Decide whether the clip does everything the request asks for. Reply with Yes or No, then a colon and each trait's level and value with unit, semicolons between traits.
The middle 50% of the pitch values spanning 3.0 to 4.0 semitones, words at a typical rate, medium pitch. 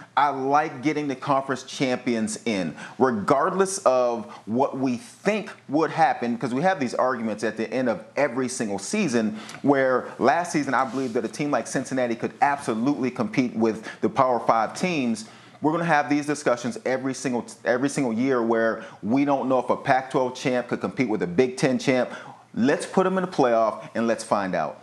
No: average, 3.4 semitones; average, 195 wpm; low, 130 Hz